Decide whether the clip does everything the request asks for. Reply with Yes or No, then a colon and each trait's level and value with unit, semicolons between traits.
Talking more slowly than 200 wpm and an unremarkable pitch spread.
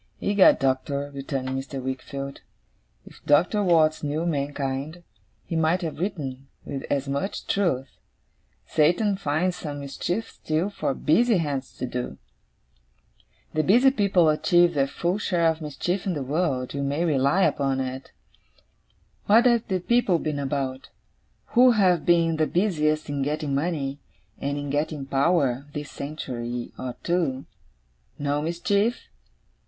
Yes: average, 140 wpm; average, 4.3 semitones